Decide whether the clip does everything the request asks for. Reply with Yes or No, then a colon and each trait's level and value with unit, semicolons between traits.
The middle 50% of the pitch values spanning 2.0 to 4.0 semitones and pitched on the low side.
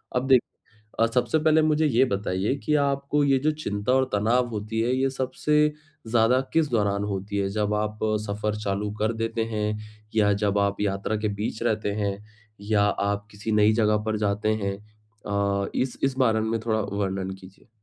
Yes: average, 3.6 semitones; low, 110 Hz